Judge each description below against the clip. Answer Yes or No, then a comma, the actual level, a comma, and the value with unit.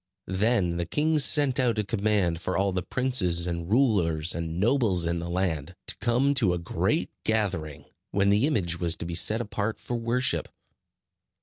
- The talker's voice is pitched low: Yes, low, 100 Hz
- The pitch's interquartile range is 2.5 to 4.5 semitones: No, wide, 5.6 semitones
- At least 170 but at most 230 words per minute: Yes, average, 180 wpm